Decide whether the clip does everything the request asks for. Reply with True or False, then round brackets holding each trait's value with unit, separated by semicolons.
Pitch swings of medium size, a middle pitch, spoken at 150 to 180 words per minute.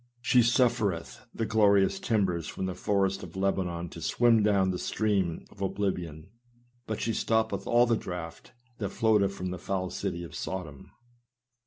False (3.5 semitones; 95 Hz; 160 wpm)